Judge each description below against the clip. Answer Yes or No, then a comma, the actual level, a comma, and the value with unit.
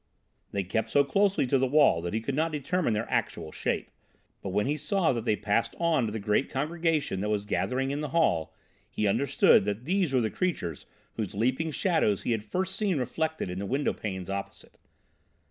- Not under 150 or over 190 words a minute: No, average, 200 wpm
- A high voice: No, low, 130 Hz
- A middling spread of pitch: No, wide, 7.4 semitones